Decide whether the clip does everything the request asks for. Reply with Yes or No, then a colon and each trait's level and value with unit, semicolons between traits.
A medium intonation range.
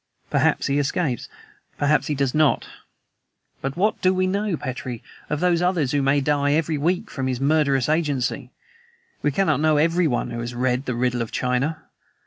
Yes: average, 3.7 semitones